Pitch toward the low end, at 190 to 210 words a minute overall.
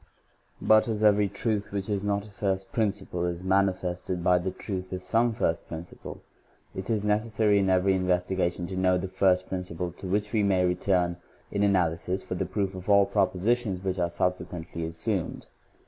Yes: very low, 95 Hz; average, 195 wpm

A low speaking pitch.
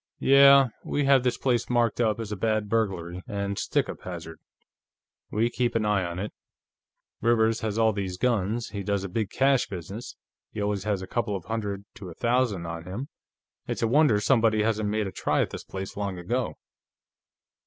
Yes: low, 105 Hz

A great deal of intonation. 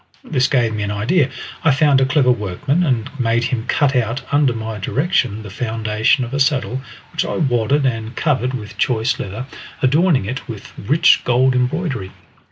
No: average, 3.8 semitones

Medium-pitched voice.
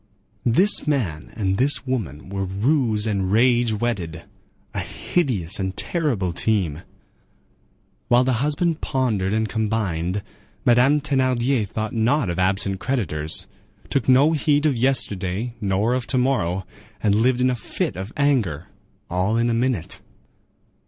No: low, 110 Hz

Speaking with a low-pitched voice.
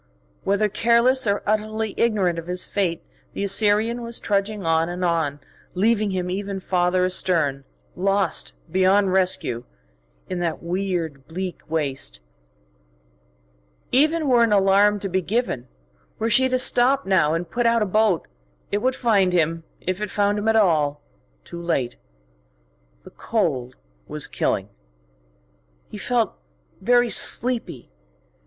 No: high, 195 Hz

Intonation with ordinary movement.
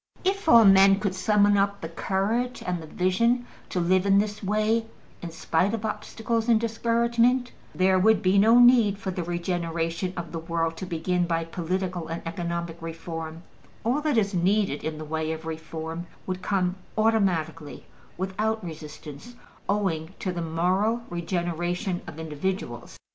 Yes: average, 4.3 semitones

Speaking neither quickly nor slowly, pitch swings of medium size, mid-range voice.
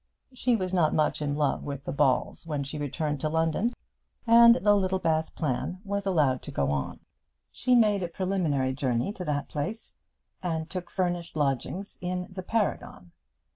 Yes: average, 170 wpm; average, 5.0 semitones; medium, 165 Hz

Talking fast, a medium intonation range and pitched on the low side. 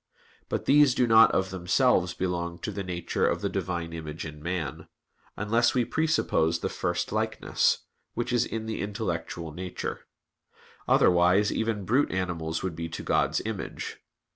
No: average, 155 wpm; average, 4.8 semitones; very low, 95 Hz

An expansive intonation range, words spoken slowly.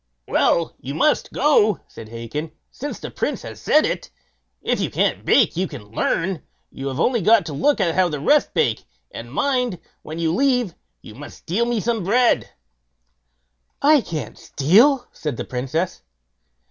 No: wide, 8.8 semitones; average, 165 wpm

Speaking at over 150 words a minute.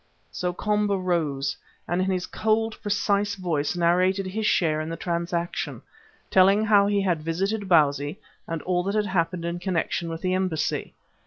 Yes: average, 165 wpm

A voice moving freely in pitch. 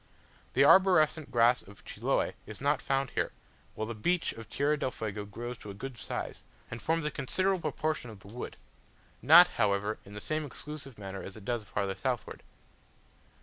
Yes: wide, 6.4 semitones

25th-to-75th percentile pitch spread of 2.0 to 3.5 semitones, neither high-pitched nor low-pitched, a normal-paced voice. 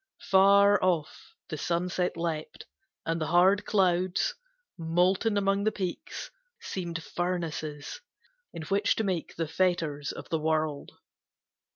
No: average, 3.0 semitones; medium, 175 Hz; slow, 120 wpm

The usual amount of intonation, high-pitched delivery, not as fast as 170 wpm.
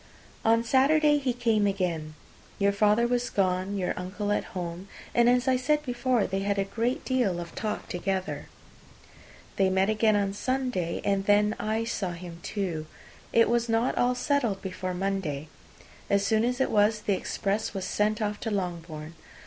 No: average, 3.9 semitones; high, 205 Hz; average, 175 wpm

